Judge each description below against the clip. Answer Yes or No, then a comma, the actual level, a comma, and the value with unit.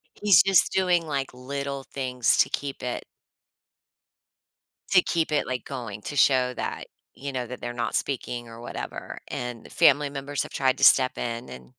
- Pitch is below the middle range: Yes, low, 130 Hz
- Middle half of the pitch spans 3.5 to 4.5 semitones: No, average, 2.7 semitones